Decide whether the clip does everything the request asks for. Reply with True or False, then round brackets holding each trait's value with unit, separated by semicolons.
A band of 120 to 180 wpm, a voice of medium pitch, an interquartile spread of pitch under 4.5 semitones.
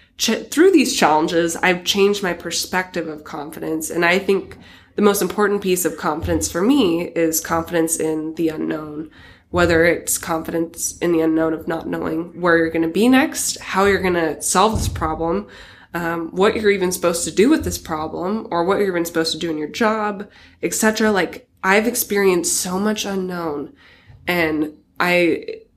True (175 wpm; 175 Hz; 3.5 semitones)